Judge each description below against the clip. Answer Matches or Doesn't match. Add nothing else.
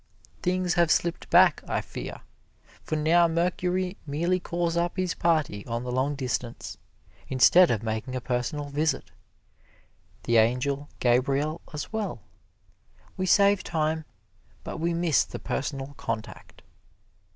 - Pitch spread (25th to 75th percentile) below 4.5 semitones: Doesn't match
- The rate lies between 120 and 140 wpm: Matches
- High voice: Doesn't match